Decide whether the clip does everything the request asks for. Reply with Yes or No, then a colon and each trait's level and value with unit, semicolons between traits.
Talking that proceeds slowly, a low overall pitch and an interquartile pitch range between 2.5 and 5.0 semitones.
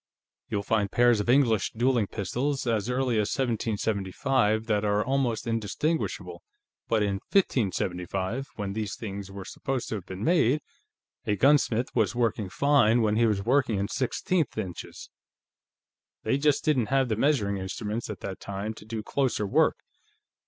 No: average, 155 wpm; low, 110 Hz; average, 4.2 semitones